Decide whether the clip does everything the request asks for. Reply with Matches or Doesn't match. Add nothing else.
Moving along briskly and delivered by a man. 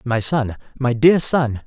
Doesn't match